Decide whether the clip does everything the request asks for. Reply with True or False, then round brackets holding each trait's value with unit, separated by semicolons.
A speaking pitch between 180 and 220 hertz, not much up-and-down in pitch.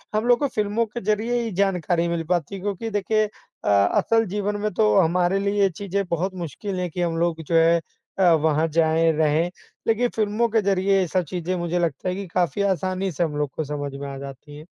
False (185 Hz; 3.9 semitones)